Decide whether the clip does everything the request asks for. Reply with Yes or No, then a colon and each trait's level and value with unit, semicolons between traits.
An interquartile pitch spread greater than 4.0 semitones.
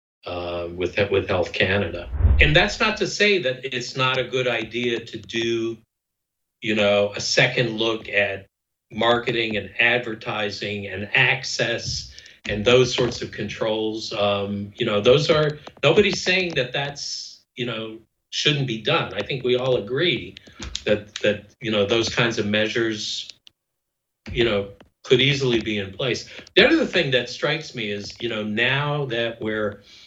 No: average, 3.5 semitones